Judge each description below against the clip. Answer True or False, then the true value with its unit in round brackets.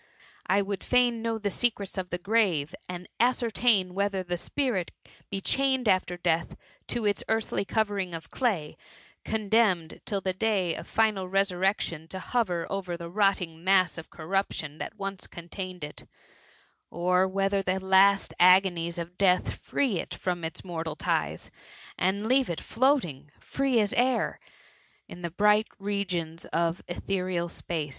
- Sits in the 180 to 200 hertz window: True (190 Hz)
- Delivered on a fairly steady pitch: False (3.3 semitones)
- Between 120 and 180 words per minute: True (155 wpm)